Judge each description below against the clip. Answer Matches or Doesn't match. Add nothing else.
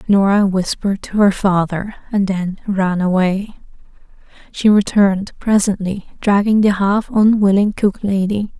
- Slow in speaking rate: Matches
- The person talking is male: Doesn't match